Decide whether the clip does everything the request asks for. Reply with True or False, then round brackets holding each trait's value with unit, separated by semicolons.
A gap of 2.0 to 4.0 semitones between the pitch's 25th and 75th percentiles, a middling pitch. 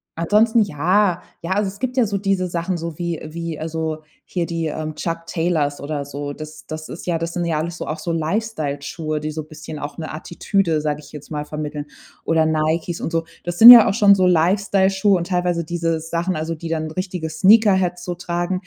True (2.9 semitones; 165 Hz)